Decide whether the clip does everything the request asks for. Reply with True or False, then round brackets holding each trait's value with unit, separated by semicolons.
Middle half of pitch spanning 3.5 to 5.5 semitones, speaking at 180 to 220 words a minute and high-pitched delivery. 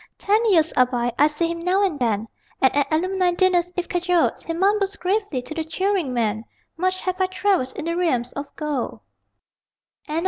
True (5.0 semitones; 185 wpm; 335 Hz)